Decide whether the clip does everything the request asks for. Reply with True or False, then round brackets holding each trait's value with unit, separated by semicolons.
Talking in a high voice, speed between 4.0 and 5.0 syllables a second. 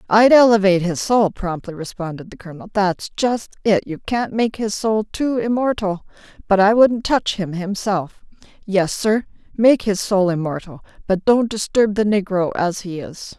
True (200 Hz; 4.6 syllables/s)